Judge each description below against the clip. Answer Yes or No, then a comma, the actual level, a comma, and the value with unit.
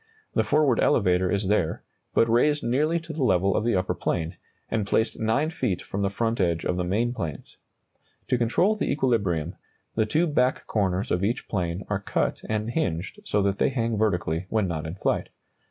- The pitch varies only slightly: No, average, 4.8 semitones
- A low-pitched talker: Yes, low, 105 Hz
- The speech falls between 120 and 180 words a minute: No, average, 195 wpm